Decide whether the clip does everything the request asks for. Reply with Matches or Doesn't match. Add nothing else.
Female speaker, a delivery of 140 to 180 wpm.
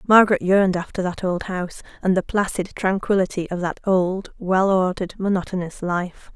Matches